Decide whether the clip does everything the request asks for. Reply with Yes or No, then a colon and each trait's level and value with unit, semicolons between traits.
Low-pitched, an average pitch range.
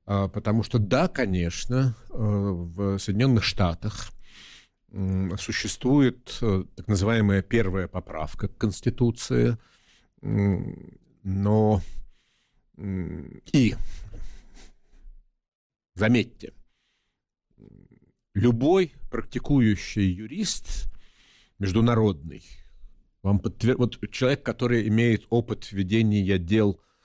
Yes: low, 105 Hz; average, 3.5 semitones